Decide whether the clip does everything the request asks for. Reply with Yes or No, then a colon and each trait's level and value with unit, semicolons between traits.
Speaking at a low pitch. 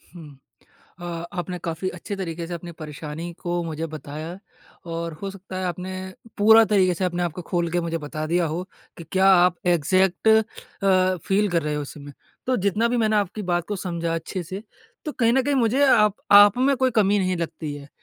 No: medium, 180 Hz